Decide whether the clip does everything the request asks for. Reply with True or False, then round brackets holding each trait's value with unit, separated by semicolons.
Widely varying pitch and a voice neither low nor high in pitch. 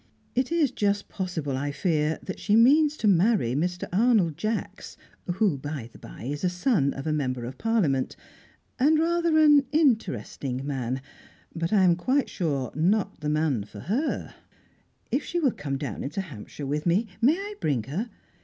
True (8.8 semitones; 175 Hz)